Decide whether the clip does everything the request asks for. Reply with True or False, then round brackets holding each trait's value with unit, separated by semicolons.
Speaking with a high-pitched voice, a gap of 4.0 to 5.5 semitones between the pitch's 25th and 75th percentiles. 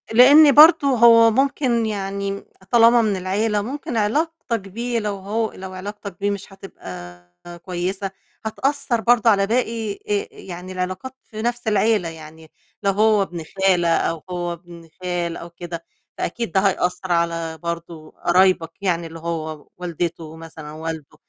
True (195 Hz; 5.1 semitones)